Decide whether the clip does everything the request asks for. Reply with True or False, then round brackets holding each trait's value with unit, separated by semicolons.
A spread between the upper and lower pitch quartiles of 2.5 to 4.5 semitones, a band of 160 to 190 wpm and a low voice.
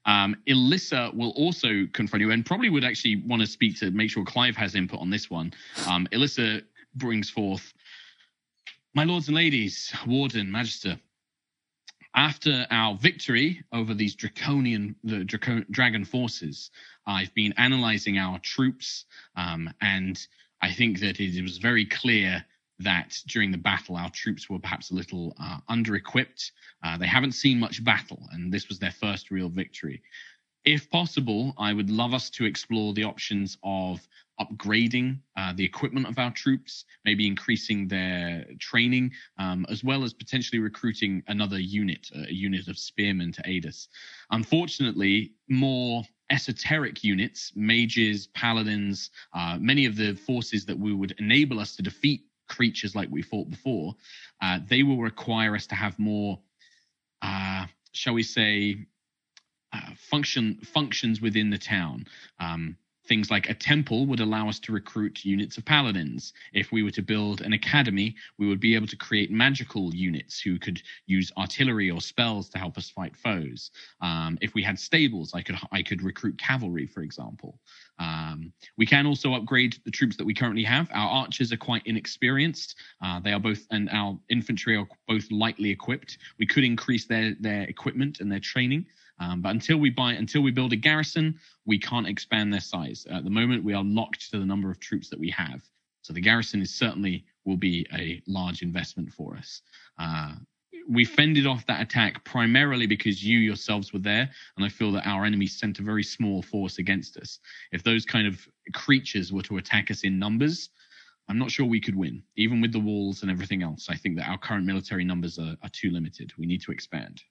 True (3.9 semitones; 180 wpm; 105 Hz)